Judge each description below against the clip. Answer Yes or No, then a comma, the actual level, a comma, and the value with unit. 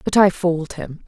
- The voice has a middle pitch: Yes, medium, 175 Hz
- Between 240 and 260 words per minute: No, fast, 225 wpm